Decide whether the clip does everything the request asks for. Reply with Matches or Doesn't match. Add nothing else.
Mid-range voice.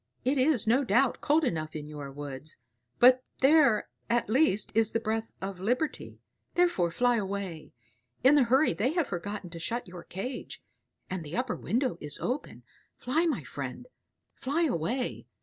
Doesn't match